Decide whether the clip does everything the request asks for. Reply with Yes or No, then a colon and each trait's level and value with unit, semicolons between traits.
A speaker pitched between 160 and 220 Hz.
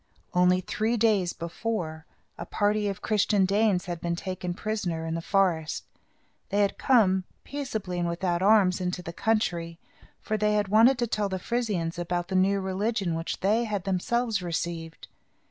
Yes: high, 190 Hz